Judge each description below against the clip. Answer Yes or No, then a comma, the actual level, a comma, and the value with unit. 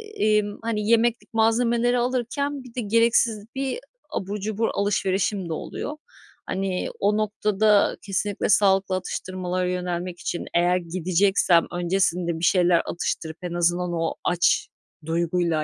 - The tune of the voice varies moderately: Yes, average, 3.6 semitones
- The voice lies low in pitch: No, high, 195 Hz